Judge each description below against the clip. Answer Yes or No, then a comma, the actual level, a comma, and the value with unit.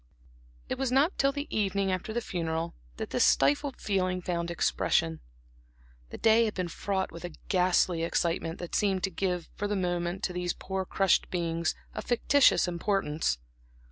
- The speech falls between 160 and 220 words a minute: Yes, average, 170 wpm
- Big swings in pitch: No, average, 3.0 semitones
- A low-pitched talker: No, medium, 185 Hz